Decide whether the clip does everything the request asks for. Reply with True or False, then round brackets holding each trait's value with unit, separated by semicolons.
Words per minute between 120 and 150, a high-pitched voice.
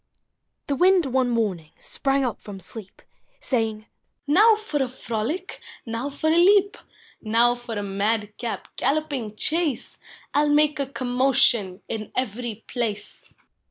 True (145 wpm; 245 Hz)